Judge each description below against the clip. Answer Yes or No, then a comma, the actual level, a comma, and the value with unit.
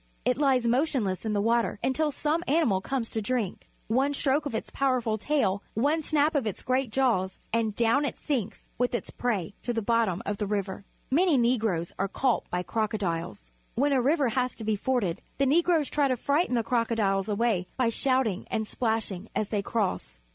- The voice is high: Yes, high, 235 Hz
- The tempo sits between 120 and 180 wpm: No, average, 195 wpm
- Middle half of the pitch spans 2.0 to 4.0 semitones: No, average, 4.6 semitones